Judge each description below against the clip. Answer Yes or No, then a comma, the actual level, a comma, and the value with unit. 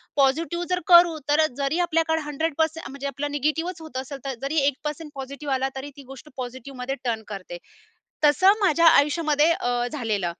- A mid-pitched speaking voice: No, very high, 290 Hz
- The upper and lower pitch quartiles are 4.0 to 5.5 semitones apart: No, average, 3.3 semitones